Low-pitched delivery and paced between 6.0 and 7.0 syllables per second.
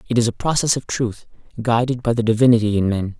Yes: low, 115 Hz; 6.3 syllables/s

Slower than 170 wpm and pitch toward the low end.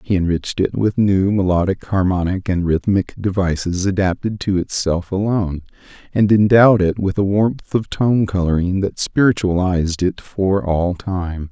Yes: average, 150 wpm; very low, 95 Hz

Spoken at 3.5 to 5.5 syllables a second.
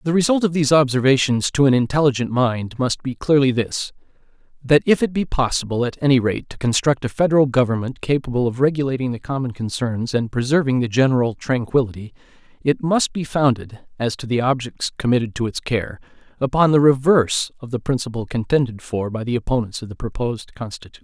No: 5.9 syllables/s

